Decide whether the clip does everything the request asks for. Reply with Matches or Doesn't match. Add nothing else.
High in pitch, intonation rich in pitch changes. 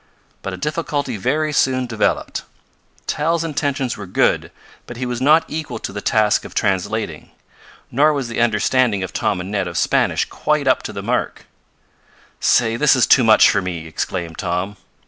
Doesn't match